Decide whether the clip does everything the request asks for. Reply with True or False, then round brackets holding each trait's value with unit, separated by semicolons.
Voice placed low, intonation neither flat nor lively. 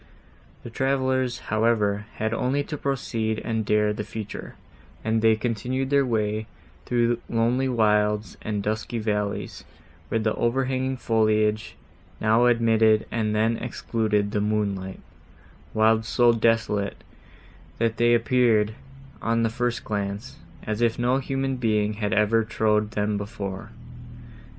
False (110 Hz; 2.1 semitones)